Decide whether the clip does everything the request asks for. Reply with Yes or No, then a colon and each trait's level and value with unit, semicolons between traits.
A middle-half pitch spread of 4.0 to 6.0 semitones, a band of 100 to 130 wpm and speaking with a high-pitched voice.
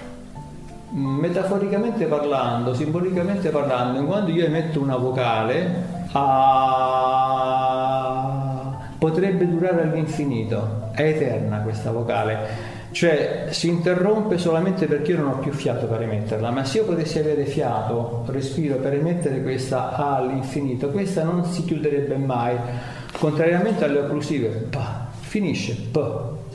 No: average, 4.8 semitones; slow, 115 wpm; medium, 140 Hz